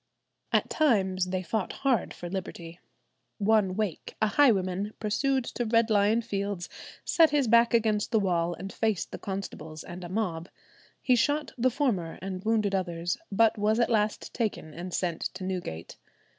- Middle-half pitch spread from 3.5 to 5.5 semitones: Yes, average, 3.8 semitones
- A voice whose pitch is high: Yes, high, 205 Hz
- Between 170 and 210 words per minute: No, average, 160 wpm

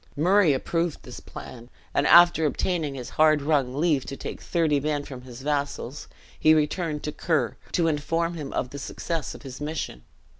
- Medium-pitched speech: Yes, medium, 150 Hz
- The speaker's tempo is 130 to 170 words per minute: No, average, 180 wpm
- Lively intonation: No, average, 3.0 semitones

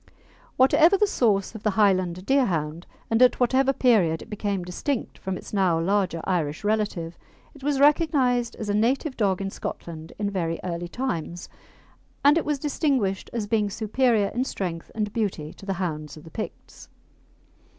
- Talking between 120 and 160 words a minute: No, average, 170 wpm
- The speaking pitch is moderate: No, high, 205 Hz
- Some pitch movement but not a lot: No, wide, 6.1 semitones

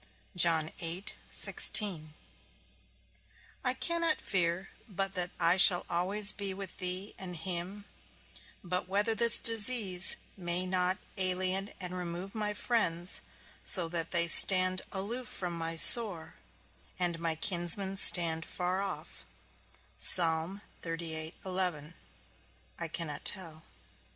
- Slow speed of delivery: Yes, slow, 100 wpm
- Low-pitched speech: No, medium, 185 Hz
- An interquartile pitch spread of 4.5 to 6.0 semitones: No, narrow, 2.5 semitones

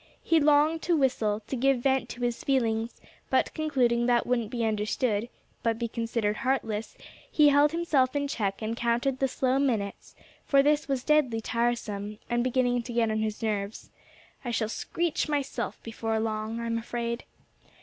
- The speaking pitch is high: Yes, high, 240 Hz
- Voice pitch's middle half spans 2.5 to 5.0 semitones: Yes, average, 3.3 semitones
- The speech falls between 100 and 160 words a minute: No, average, 170 wpm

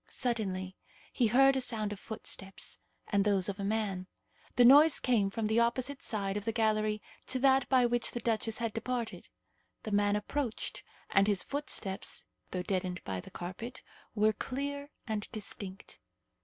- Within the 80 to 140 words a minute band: No, average, 165 wpm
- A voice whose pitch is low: No, high, 220 Hz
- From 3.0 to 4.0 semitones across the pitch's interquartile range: Yes, average, 3.6 semitones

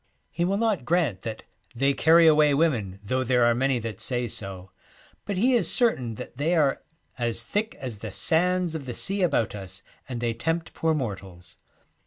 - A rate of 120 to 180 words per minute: No, average, 195 wpm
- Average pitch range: No, wide, 6.6 semitones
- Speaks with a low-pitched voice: Yes, low, 130 Hz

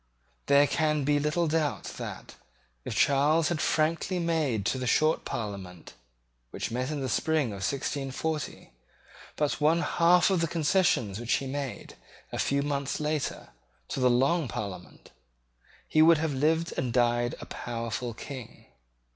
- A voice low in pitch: No, medium, 145 Hz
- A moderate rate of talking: Yes, average, 150 wpm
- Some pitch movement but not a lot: Yes, average, 4.5 semitones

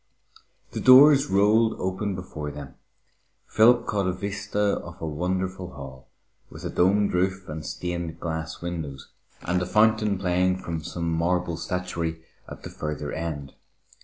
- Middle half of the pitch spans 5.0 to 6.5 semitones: No, average, 3.6 semitones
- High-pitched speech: No, very low, 90 Hz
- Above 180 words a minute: No, average, 145 wpm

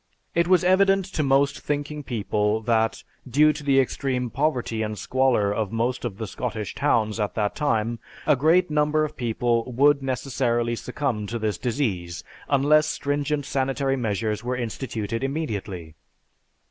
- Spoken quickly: No, average, 150 wpm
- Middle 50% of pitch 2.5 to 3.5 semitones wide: No, average, 4.6 semitones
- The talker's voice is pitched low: Yes, low, 125 Hz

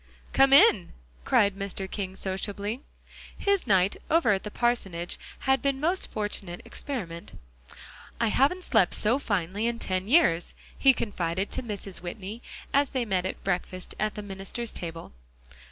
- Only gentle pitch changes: No, average, 4.8 semitones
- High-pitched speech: Yes, high, 205 Hz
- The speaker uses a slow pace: No, average, 155 wpm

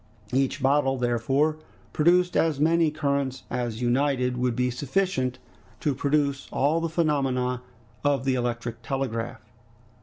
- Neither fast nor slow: No, slow, 125 wpm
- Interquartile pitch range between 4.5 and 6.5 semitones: No, average, 3.0 semitones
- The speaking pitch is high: No, low, 135 Hz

